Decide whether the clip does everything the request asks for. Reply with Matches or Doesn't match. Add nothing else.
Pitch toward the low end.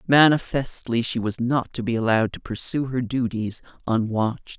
Matches